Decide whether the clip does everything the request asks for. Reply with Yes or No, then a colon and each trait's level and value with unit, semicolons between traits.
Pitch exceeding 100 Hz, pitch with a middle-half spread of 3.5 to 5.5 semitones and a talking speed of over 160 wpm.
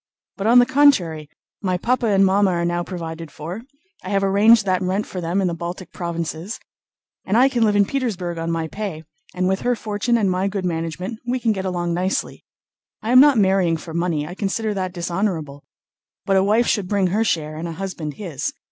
Yes: high, 190 Hz; average, 3.9 semitones; average, 200 wpm